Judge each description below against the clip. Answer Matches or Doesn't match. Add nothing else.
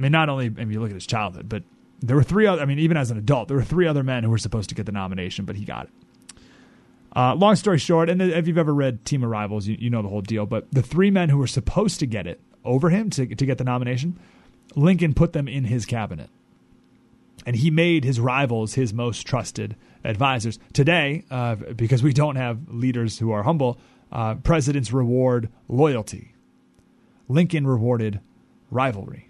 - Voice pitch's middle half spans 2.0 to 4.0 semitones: Doesn't match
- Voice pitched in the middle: Doesn't match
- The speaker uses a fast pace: Matches